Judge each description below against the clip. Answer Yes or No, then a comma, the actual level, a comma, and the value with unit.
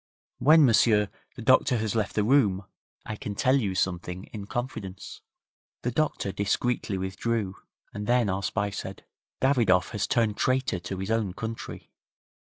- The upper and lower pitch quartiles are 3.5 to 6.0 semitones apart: Yes, average, 4.0 semitones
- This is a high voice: No, low, 105 Hz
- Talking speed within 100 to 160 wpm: Yes, average, 155 wpm